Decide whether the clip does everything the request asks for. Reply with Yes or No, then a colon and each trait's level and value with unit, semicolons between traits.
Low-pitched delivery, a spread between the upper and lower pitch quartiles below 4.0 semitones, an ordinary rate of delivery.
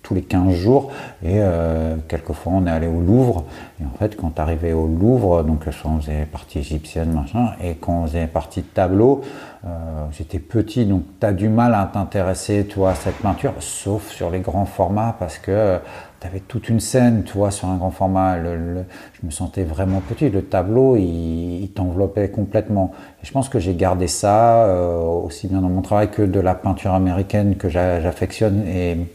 Yes: very low, 95 Hz; average, 3.3 semitones; average, 205 wpm